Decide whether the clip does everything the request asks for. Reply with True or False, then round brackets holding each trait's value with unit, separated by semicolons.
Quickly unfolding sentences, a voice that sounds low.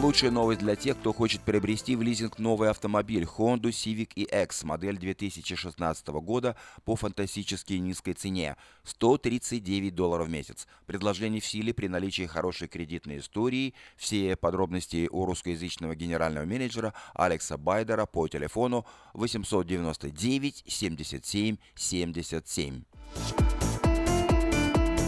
False (110 wpm; 100 Hz)